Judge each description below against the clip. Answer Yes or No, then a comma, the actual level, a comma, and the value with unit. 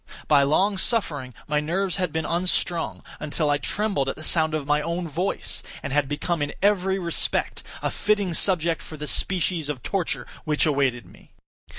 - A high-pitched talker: No, medium, 160 Hz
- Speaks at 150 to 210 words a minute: Yes, average, 180 wpm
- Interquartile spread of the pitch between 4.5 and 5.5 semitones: No, average, 3.8 semitones